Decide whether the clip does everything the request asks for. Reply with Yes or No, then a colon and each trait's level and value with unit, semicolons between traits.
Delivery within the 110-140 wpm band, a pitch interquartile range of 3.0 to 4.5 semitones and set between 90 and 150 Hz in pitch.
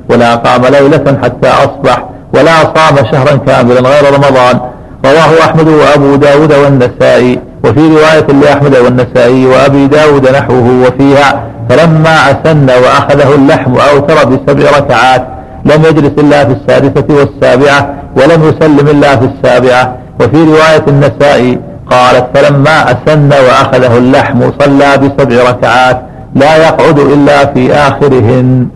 No: average, 120 wpm; narrow, 2.6 semitones; medium, 140 Hz